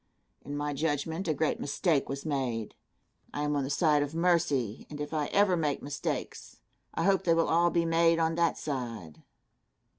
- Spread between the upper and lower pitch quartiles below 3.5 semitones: Yes, average, 2.8 semitones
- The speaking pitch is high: No, medium, 150 Hz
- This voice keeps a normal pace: Yes, average, 185 wpm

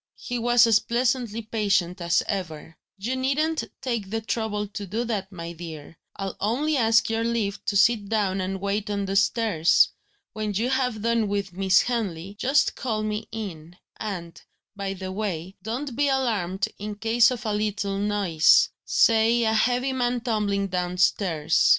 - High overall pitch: Yes, high, 210 Hz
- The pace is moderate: Yes, average, 165 wpm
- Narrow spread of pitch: No, average, 3.3 semitones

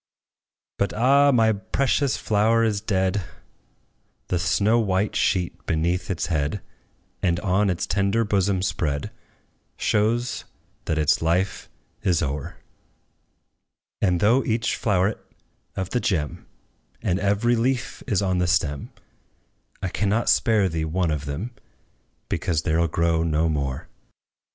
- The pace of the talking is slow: Yes, slow, 130 wpm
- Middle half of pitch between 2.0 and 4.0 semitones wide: No, average, 4.6 semitones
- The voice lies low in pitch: Yes, very low, 95 Hz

